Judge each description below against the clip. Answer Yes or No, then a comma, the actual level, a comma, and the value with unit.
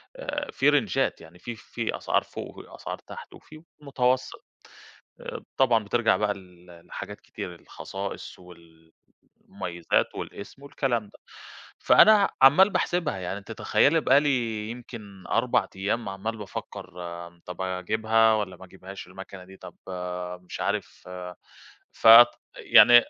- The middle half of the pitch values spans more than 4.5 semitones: Yes, average, 5.1 semitones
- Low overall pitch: Yes, low, 100 Hz